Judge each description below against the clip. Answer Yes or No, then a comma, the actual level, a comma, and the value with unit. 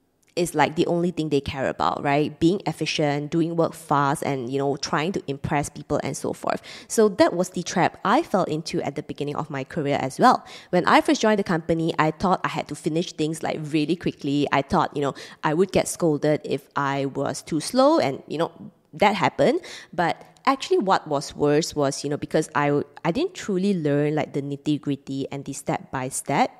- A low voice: No, medium, 150 Hz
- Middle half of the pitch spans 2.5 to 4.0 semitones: Yes, average, 3.6 semitones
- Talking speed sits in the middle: No, fast, 210 wpm